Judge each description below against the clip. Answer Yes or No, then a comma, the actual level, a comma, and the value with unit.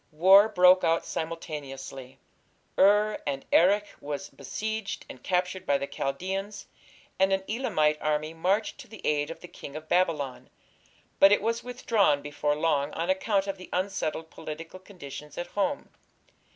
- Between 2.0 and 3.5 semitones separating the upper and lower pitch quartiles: No, average, 4.9 semitones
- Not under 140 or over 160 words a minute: Yes, average, 150 wpm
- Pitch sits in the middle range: Yes, medium, 175 Hz